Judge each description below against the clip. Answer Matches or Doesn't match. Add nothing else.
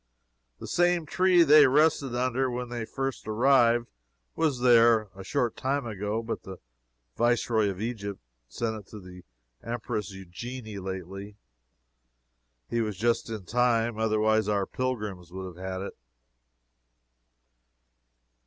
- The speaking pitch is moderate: Doesn't match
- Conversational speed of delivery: Doesn't match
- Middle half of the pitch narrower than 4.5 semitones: Matches